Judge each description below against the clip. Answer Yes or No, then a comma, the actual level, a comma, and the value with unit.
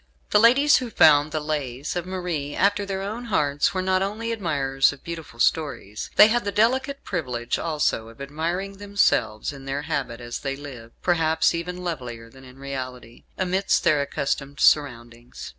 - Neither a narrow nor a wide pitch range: No, wide, 5.8 semitones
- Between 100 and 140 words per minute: No, average, 170 wpm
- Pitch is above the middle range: No, medium, 150 Hz